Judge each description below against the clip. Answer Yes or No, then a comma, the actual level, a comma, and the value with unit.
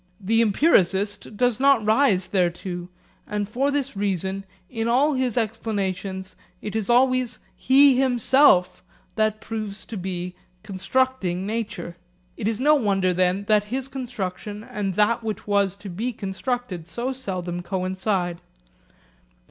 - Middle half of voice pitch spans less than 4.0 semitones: No, average, 4.5 semitones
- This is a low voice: No, high, 210 Hz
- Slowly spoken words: Yes, slow, 130 wpm